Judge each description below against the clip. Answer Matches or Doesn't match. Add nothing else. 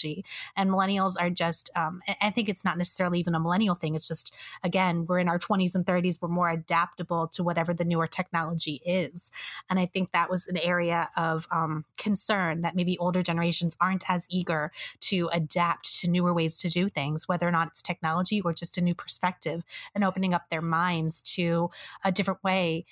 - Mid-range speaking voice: Matches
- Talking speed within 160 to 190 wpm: Doesn't match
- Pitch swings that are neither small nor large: Doesn't match